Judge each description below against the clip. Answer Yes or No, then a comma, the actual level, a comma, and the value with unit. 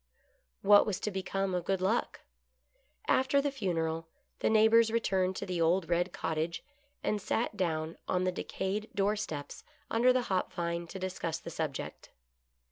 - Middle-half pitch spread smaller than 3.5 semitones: No, average, 3.9 semitones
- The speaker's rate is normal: Yes, average, 160 wpm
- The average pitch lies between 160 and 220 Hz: Yes, high, 190 Hz